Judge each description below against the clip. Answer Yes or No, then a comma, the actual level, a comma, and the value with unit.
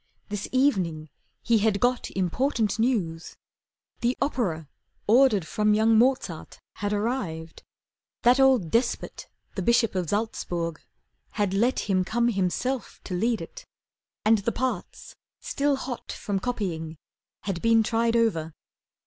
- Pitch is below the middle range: No, high, 220 Hz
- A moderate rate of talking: No, slow, 130 wpm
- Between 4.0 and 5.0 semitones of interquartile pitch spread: Yes, average, 4.7 semitones